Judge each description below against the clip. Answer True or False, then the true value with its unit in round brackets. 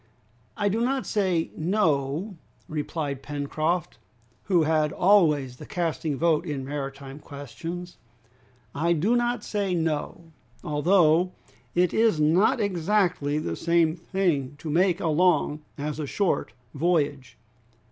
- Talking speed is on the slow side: True (125 wpm)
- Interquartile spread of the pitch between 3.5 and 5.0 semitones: True (3.8 semitones)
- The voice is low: False (165 Hz)